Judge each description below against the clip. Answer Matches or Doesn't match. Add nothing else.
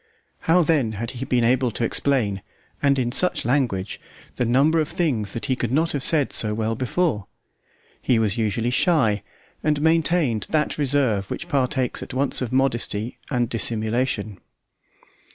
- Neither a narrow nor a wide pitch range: Matches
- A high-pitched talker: Doesn't match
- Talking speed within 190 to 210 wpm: Doesn't match